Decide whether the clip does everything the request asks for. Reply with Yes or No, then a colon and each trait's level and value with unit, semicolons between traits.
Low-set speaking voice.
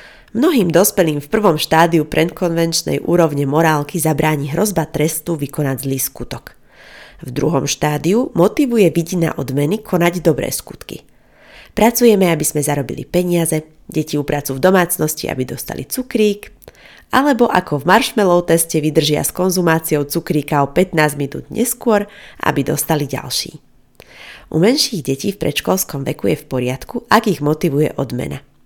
No: medium, 160 Hz